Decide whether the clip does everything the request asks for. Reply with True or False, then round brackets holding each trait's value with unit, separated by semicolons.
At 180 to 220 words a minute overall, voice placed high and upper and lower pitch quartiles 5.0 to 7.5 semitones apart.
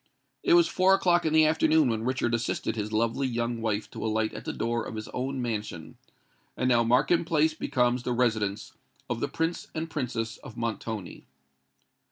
False (185 wpm; 120 Hz; 5.6 semitones)